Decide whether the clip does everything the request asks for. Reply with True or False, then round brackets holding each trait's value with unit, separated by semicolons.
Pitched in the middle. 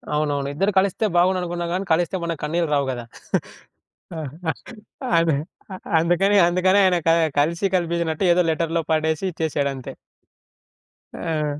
True (165 Hz)